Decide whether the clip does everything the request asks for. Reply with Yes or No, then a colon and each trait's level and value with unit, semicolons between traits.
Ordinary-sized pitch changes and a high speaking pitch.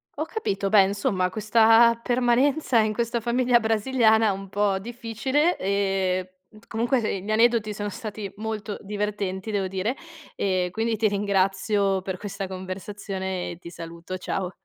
Yes: average, 3.1 semitones; high, 205 Hz